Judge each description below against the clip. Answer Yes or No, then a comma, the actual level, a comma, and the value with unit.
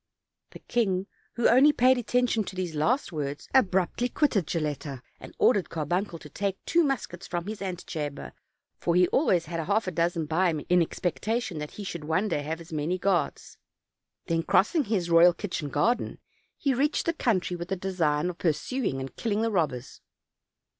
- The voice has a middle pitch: Yes, medium, 180 Hz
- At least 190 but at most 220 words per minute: No, average, 180 wpm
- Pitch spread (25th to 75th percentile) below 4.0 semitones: No, average, 5.3 semitones